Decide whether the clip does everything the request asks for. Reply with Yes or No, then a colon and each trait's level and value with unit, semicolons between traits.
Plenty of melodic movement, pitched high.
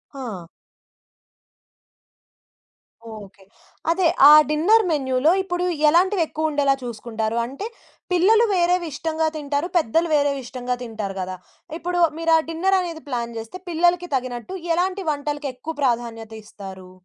Yes: wide, 6.3 semitones; very high, 295 Hz